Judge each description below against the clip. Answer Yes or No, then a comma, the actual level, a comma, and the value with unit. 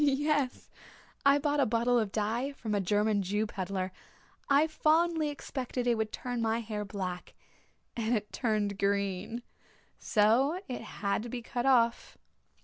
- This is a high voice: Yes, high, 230 Hz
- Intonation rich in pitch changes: No, average, 4.5 semitones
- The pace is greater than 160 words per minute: No, average, 155 wpm